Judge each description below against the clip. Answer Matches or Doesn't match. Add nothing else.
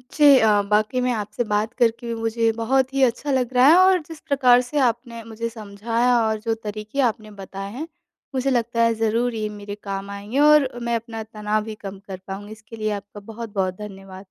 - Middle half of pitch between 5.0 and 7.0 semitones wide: Doesn't match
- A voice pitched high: Matches